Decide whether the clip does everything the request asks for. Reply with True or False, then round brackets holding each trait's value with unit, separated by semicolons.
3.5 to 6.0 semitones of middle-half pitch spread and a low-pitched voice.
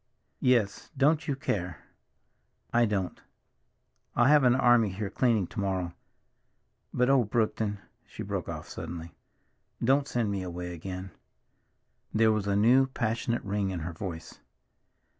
True (4.5 semitones; 105 Hz)